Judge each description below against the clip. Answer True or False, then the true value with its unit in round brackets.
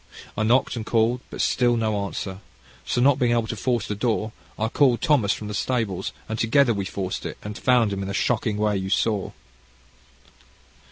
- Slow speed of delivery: False (200 wpm)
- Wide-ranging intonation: False (3.0 semitones)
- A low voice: True (110 Hz)